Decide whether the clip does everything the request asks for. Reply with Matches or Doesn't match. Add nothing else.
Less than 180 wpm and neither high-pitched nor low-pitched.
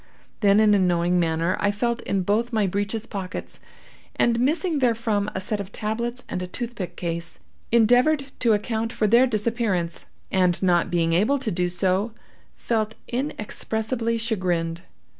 Doesn't match